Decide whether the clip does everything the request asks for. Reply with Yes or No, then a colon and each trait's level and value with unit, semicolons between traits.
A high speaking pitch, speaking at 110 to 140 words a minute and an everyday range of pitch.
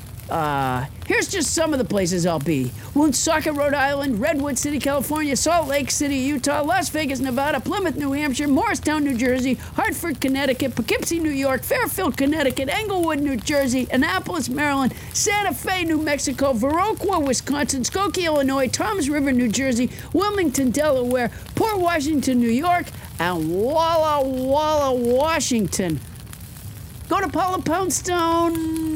Yes: very high, 290 Hz; slow, 135 wpm; average, 3.8 semitones